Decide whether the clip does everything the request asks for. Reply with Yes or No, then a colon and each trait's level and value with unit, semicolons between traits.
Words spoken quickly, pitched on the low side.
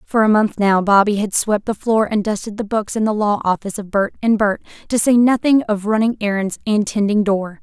No: fast, 235 wpm; high, 210 Hz